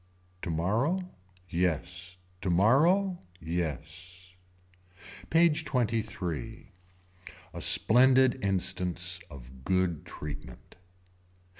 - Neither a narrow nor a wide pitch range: No, wide, 6.2 semitones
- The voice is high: No, very low, 95 Hz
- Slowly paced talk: Yes, slow, 60 wpm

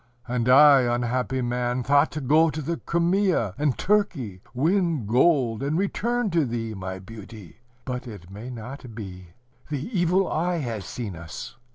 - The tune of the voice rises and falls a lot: Yes, wide, 6.2 semitones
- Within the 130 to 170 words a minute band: Yes, average, 160 wpm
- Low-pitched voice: Yes, low, 125 Hz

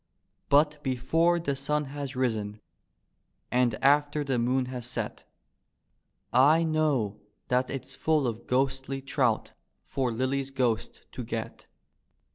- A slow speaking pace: Yes, slow, 120 wpm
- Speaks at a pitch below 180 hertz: Yes, low, 135 Hz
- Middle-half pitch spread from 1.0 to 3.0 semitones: Yes, narrow, 2.6 semitones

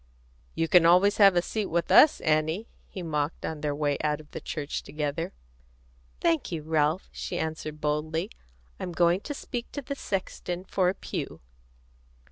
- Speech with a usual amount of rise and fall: Yes, average, 3.4 semitones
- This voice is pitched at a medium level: Yes, medium, 165 Hz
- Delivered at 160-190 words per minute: Yes, average, 170 wpm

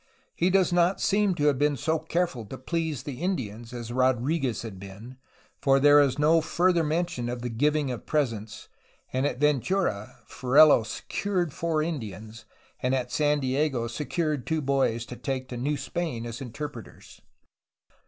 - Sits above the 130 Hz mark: Yes, medium, 140 Hz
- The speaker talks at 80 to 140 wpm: No, average, 165 wpm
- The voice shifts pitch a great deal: No, average, 4.7 semitones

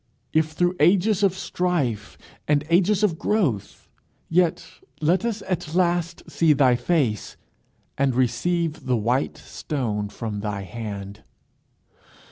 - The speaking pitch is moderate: Yes, medium, 155 Hz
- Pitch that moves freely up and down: Yes, wide, 7.0 semitones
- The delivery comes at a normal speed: No, slow, 120 wpm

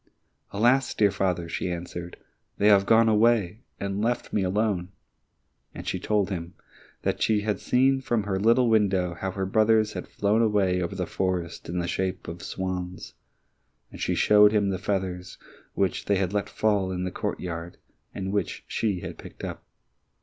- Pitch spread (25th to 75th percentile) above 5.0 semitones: No, average, 2.8 semitones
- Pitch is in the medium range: No, low, 100 Hz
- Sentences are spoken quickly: No, average, 175 wpm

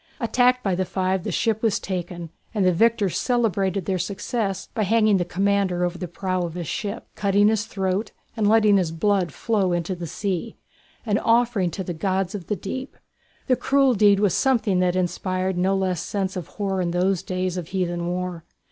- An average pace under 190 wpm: No, average, 195 wpm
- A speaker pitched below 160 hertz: No, high, 190 Hz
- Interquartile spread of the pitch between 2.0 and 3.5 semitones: Yes, narrow, 2.6 semitones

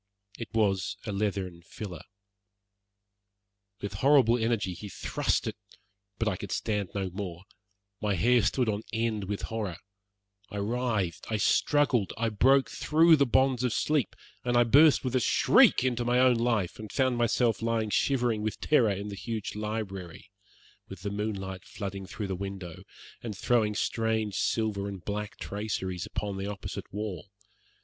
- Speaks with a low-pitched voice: Yes, low, 105 Hz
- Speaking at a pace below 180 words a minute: Yes, average, 160 wpm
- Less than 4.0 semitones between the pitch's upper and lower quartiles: Yes, average, 3.3 semitones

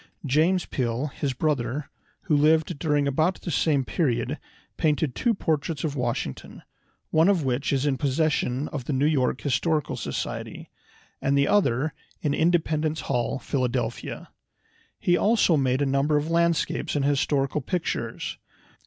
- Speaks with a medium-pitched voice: Yes, medium, 145 Hz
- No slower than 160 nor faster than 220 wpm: No, average, 145 wpm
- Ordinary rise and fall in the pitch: Yes, average, 3.0 semitones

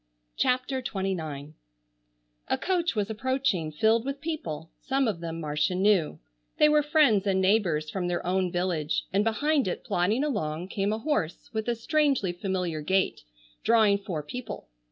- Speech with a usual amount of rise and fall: No, wide, 6.8 semitones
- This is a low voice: No, high, 195 Hz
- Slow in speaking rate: No, average, 155 wpm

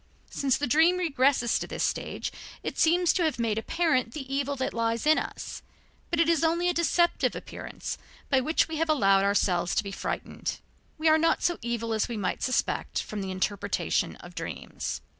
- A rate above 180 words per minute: Yes, average, 195 wpm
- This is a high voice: Yes, very high, 275 Hz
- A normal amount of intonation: No, wide, 6.2 semitones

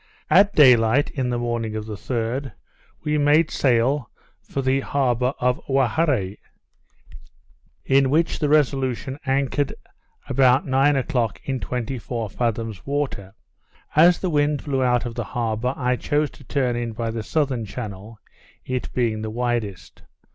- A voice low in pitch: Yes, low, 125 Hz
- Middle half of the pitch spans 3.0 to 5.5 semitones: Yes, average, 3.4 semitones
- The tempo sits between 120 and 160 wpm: Yes, average, 150 wpm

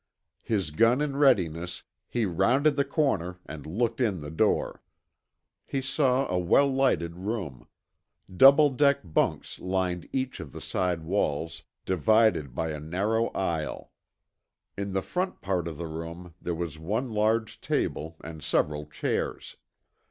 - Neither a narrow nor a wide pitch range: No, wide, 6.9 semitones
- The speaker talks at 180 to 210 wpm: No, average, 145 wpm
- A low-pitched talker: Yes, very low, 95 Hz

